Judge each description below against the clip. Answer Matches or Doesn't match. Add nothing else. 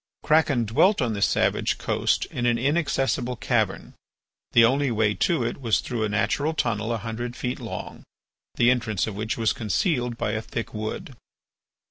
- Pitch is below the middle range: Matches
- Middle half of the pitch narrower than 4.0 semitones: Matches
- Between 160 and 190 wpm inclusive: Matches